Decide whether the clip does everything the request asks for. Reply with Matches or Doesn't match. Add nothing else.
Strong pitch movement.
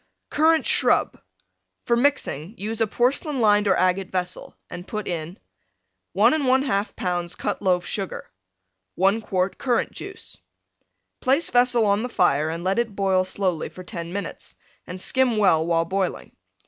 Doesn't match